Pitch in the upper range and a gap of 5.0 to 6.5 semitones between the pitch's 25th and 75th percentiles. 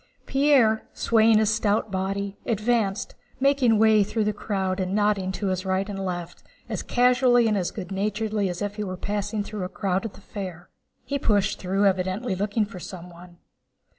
No: high, 205 Hz; narrow, 2.5 semitones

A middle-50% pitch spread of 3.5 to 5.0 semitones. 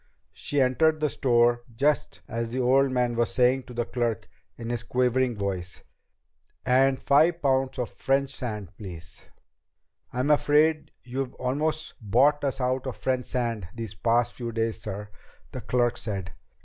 No: average, 2.7 semitones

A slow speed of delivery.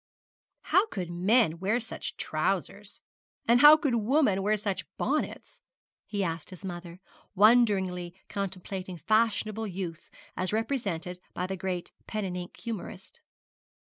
Yes: slow, 130 wpm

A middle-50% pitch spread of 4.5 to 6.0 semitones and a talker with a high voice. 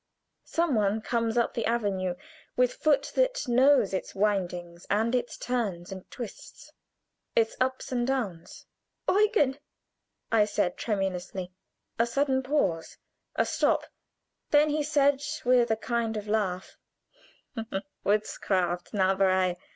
Yes: average, 5.3 semitones; high, 225 Hz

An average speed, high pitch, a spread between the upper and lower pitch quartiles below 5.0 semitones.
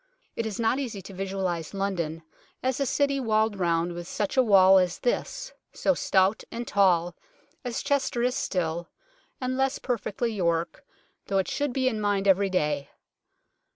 No: average, 165 wpm; high, 200 Hz; average, 5.3 semitones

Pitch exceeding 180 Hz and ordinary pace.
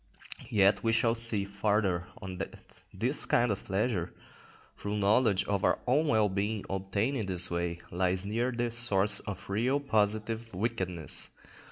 No: low, 105 Hz; average, 165 wpm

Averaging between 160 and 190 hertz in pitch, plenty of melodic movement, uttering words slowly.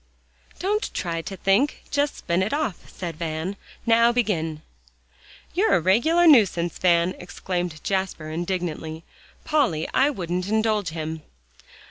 Yes: medium, 185 Hz; wide, 5.7 semitones; slow, 125 wpm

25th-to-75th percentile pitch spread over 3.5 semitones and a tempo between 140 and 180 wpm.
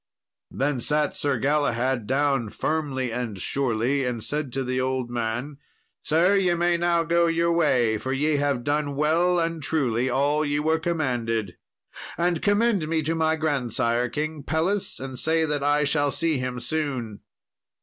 Yes: average, 4.0 semitones; average, 160 wpm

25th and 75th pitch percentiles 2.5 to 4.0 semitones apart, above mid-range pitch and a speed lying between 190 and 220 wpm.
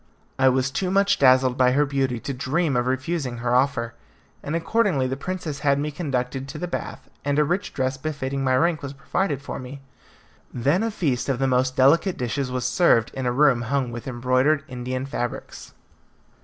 No: average, 2.8 semitones; low, 135 Hz; average, 195 wpm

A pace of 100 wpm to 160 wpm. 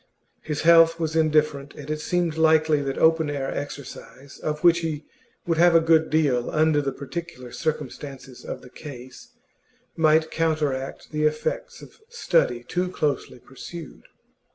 Yes: average, 150 wpm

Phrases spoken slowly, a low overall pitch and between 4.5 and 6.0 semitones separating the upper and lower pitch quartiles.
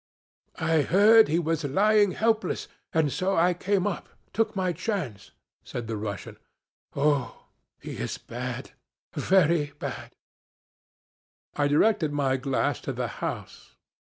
No: slow, 130 wpm; medium, 165 Hz; wide, 5.4 semitones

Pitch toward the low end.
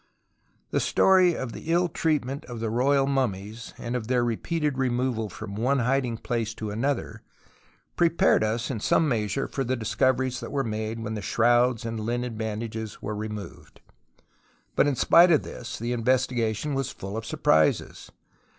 Yes: low, 120 Hz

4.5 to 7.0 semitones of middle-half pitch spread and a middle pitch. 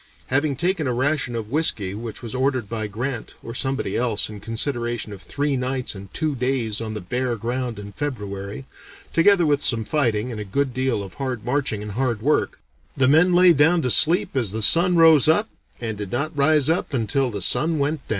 No: average, 4.9 semitones; low, 130 Hz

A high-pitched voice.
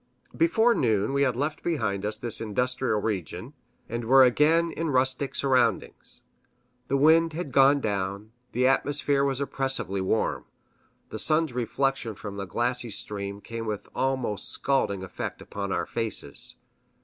No: low, 125 Hz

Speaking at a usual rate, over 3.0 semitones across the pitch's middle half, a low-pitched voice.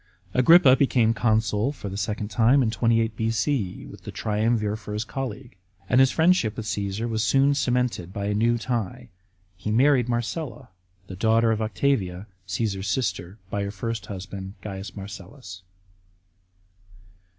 Yes: average, 150 wpm; average, 3.5 semitones; low, 110 Hz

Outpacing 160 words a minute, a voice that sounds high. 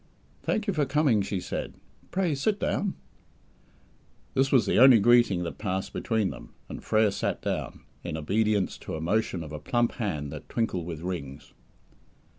No: average, 170 wpm; low, 105 Hz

